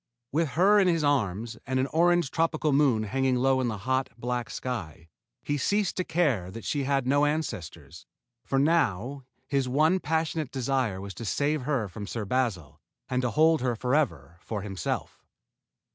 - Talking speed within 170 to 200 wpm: Yes, average, 175 wpm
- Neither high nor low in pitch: No, low, 130 Hz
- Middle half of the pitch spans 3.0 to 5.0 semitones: No, wide, 5.6 semitones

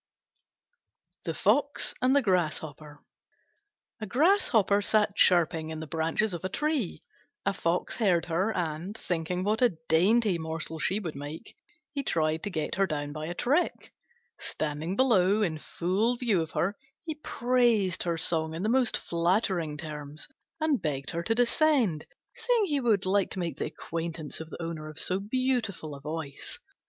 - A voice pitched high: No, medium, 180 Hz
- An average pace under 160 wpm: No, average, 165 wpm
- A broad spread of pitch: Yes, wide, 5.7 semitones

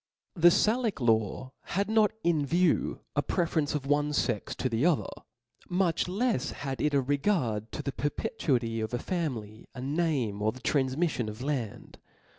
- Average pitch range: No, wide, 6.0 semitones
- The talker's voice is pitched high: No, medium, 145 Hz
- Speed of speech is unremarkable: Yes, average, 190 wpm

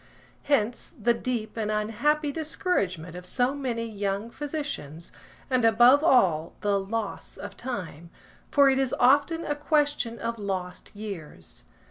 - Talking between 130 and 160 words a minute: Yes, slow, 135 wpm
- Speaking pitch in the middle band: No, high, 230 Hz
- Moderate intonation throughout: No, wide, 6.0 semitones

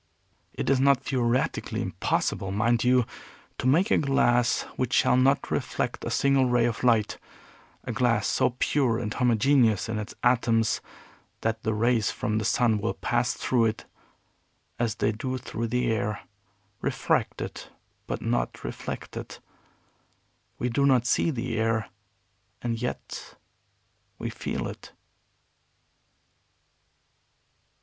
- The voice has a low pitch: Yes, low, 120 Hz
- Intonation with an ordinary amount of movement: No, narrow, 2.3 semitones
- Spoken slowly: Yes, slow, 130 wpm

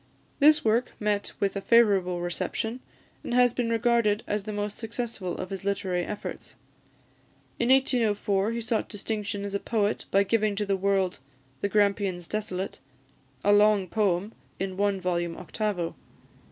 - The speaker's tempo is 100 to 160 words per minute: Yes, average, 155 wpm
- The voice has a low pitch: No, high, 205 Hz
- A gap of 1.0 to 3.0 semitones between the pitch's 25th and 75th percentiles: Yes, narrow, 2.5 semitones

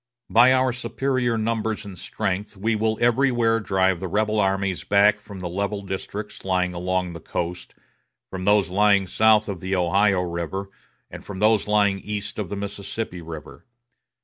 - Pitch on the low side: Yes, low, 100 Hz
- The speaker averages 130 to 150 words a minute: No, average, 165 wpm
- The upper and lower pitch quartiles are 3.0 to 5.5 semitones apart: No, narrow, 2.6 semitones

